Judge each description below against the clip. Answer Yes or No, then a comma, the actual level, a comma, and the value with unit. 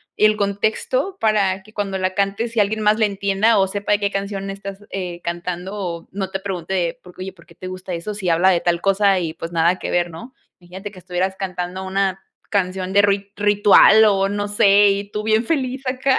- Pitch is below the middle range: No, high, 195 Hz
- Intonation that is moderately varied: No, narrow, 1.9 semitones